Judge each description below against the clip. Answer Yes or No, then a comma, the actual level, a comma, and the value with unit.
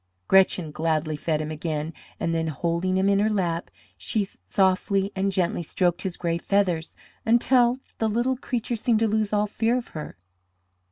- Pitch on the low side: No, high, 190 Hz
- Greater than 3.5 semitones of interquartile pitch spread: Yes, average, 4.6 semitones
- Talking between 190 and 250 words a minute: No, average, 170 wpm